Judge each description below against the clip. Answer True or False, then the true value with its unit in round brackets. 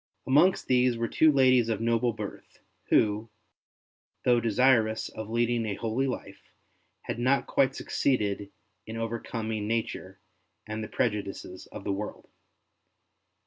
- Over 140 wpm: False (135 wpm)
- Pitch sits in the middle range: False (115 Hz)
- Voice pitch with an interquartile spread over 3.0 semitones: False (2.7 semitones)